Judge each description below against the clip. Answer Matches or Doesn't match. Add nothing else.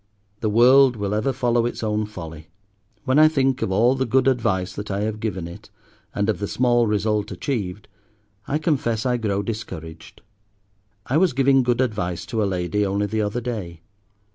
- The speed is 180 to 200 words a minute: Matches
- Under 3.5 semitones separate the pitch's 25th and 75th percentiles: Doesn't match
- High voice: Doesn't match